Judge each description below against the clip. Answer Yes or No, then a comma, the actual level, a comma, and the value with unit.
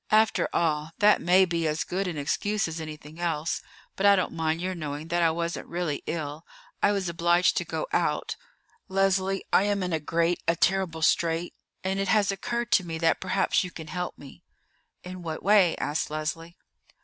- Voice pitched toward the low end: No, medium, 175 Hz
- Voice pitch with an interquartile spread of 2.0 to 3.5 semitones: Yes, average, 3.0 semitones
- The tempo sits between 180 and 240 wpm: Yes, average, 195 wpm